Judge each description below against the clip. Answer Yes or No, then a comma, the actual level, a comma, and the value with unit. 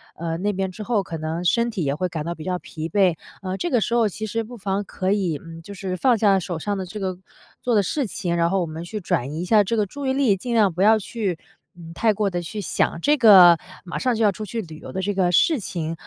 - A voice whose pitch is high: Yes, high, 195 Hz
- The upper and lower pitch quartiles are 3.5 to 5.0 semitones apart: Yes, average, 4.1 semitones